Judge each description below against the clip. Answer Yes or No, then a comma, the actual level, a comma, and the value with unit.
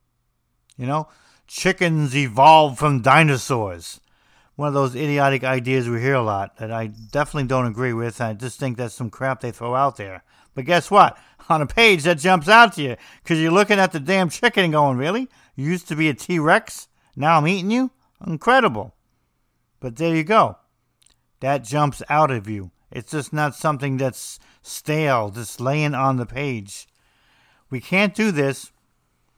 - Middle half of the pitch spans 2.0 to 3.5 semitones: No, average, 4.6 semitones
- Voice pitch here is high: No, medium, 140 Hz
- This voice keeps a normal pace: Yes, average, 180 wpm